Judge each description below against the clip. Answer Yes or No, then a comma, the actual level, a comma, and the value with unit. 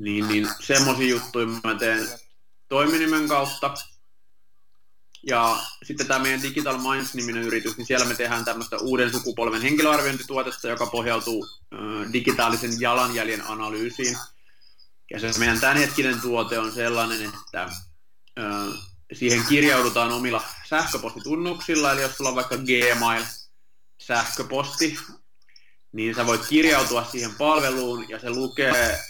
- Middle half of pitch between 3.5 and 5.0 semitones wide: No, average, 2.9 semitones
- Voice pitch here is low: Yes, low, 120 Hz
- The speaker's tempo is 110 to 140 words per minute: Yes, average, 120 wpm